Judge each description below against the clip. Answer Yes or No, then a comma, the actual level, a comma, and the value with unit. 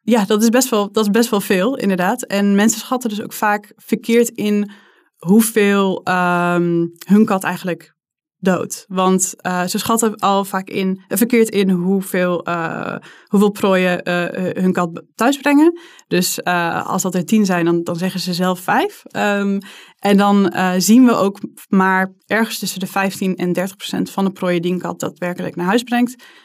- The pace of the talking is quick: No, average, 185 wpm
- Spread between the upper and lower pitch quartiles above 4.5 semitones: No, average, 3.3 semitones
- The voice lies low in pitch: No, high, 195 Hz